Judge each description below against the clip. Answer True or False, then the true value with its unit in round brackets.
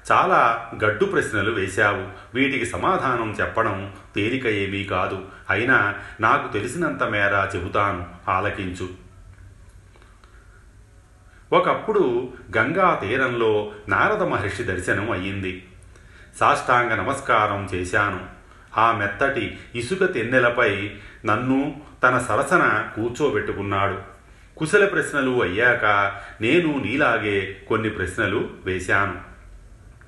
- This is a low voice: True (100 Hz)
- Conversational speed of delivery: True (85 wpm)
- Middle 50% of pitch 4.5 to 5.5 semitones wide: False (2.9 semitones)